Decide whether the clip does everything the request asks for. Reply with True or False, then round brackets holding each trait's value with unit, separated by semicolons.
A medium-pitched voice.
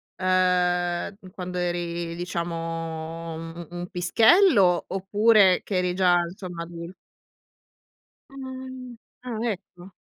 True (180 Hz)